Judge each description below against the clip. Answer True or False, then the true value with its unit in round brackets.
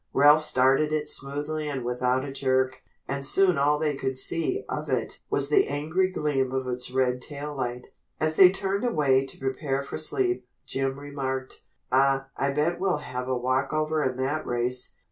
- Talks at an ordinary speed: True (180 wpm)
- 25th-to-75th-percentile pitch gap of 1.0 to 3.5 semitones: True (2.8 semitones)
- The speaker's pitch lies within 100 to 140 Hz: True (135 Hz)